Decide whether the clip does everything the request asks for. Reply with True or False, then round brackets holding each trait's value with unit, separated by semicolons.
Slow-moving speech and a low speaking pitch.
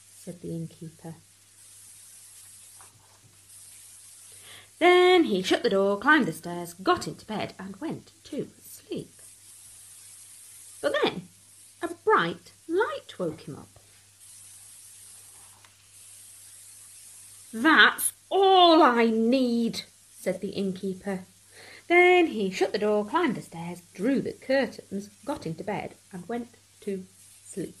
False (110 wpm; 165 Hz)